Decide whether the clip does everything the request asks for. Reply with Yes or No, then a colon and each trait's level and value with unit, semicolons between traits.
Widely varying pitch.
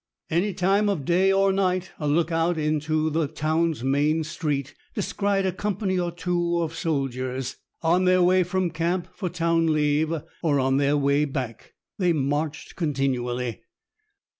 No: average, 3.8 semitones